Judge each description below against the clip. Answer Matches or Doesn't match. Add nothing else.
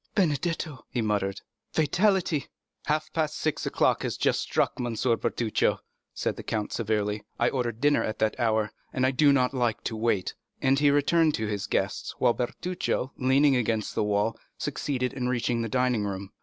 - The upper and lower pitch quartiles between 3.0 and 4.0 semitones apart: Doesn't match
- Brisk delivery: Doesn't match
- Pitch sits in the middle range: Doesn't match